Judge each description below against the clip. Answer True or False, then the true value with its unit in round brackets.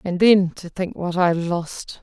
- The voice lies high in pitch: False (180 Hz)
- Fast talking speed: True (210 wpm)